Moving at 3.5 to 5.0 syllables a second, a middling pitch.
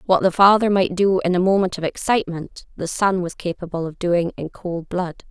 No: 5.3 syllables/s; medium, 180 Hz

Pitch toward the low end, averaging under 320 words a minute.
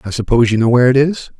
Yes: low, 125 Hz; fast, 300 wpm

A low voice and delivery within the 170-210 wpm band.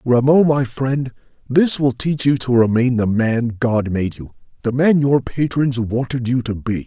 Yes: low, 125 Hz; average, 190 wpm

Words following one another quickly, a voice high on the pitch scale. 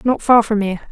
Yes: fast, 265 wpm; high, 220 Hz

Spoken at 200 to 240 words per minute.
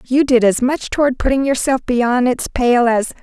Yes: fast, 205 wpm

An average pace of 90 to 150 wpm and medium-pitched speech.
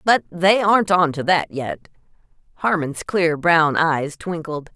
Yes: average, 140 wpm; medium, 165 Hz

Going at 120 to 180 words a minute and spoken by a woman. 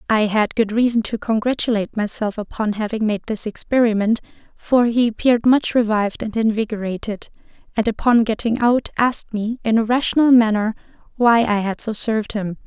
Yes: average, 165 wpm; female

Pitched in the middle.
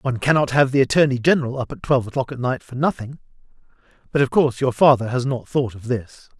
No: low, 130 Hz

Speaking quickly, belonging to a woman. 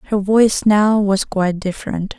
No: average, 165 wpm; female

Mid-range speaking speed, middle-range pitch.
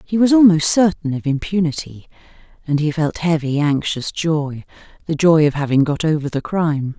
Yes: average, 170 wpm; medium, 155 Hz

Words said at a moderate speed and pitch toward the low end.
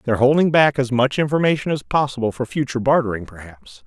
Yes: average, 185 wpm; low, 130 Hz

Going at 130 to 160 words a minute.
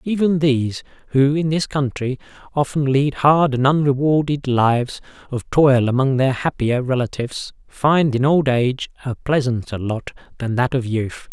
Yes: average, 155 wpm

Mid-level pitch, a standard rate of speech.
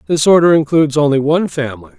Yes: medium, 150 Hz; average, 180 wpm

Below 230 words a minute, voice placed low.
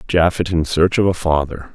Yes: fast, 205 wpm; very low, 85 Hz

